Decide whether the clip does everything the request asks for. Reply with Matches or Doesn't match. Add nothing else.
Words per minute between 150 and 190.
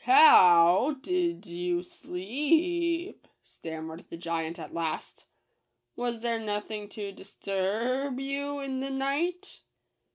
Matches